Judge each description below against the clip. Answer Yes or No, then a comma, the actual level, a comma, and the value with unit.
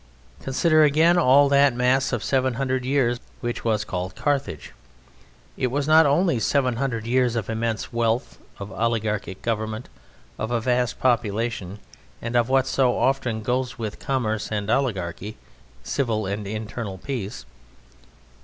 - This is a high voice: No, low, 120 Hz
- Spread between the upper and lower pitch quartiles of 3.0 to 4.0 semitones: Yes, average, 3.4 semitones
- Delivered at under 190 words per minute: Yes, average, 145 wpm